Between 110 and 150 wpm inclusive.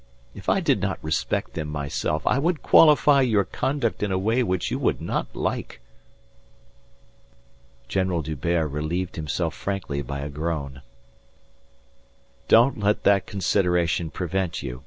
Yes: slow, 135 wpm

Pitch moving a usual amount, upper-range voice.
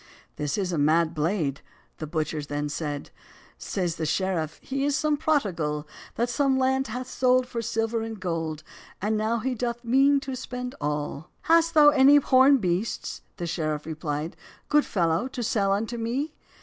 No: wide, 8.4 semitones; high, 215 Hz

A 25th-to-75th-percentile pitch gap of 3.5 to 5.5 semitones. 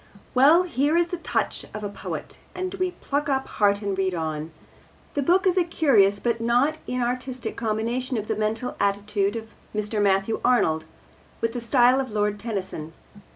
Yes: average, 5.0 semitones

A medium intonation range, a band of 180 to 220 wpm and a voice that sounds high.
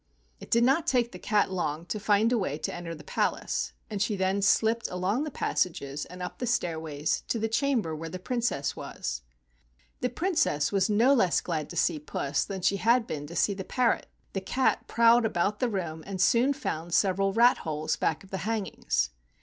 No: wide, 6.0 semitones; fast, 205 wpm; high, 195 Hz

